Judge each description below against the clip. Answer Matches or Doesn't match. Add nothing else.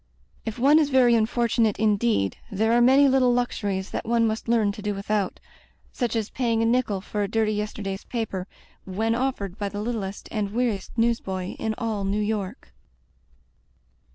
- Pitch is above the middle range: Matches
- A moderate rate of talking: Matches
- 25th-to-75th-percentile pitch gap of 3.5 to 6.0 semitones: Doesn't match